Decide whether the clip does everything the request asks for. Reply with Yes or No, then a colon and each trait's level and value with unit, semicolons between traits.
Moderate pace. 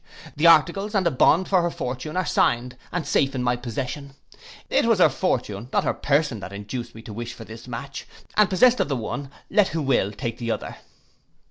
No: fast, 215 wpm